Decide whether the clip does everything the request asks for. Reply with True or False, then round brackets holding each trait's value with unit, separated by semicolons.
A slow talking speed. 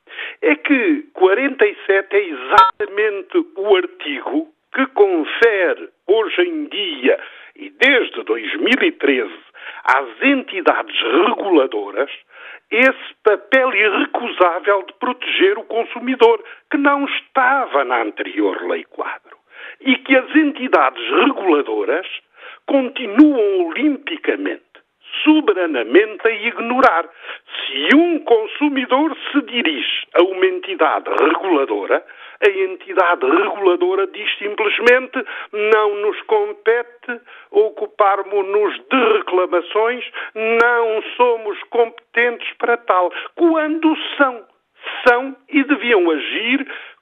True (95 wpm)